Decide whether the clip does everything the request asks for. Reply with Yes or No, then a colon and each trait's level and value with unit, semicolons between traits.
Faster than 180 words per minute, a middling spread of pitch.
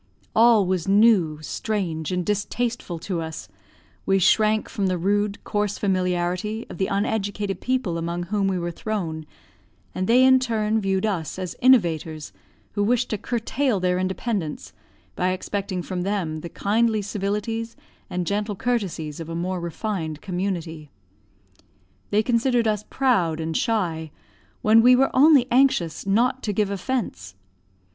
No: average, 145 wpm; average, 4.1 semitones